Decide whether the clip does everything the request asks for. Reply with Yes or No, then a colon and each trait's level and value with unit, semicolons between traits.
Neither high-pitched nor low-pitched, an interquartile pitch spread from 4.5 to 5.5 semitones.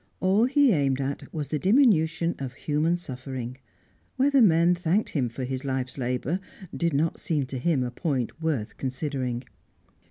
Yes: medium, 145 Hz; average, 4.9 semitones